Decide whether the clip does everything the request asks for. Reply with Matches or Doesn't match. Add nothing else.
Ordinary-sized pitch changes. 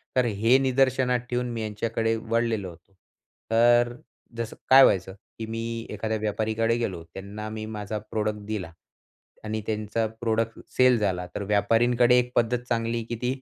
Doesn't match